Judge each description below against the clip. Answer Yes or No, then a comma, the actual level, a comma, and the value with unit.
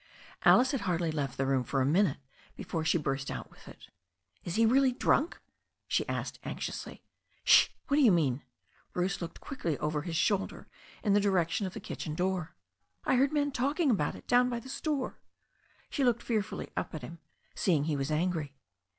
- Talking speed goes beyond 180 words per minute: Yes, average, 190 wpm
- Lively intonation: Yes, wide, 8.2 semitones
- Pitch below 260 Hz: Yes, medium, 185 Hz